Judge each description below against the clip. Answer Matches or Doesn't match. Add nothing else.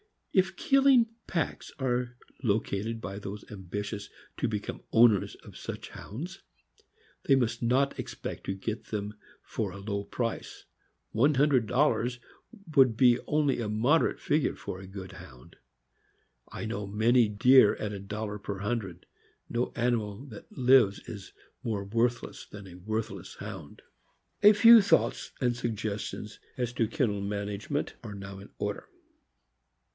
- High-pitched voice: Doesn't match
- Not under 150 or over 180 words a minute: Doesn't match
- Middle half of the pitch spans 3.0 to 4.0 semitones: Matches